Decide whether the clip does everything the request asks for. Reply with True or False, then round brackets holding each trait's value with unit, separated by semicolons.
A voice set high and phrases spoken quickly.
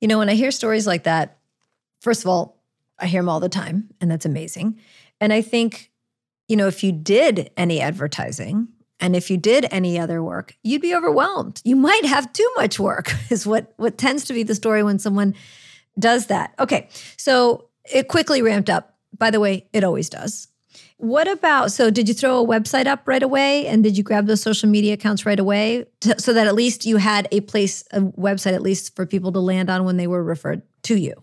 True (210 Hz; 220 wpm)